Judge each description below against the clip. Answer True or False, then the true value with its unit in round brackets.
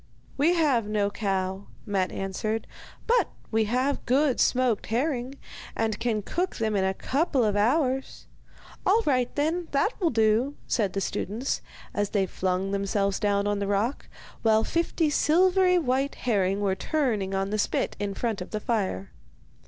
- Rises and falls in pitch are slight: False (5.6 semitones)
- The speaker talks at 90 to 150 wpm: False (160 wpm)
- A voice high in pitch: True (225 Hz)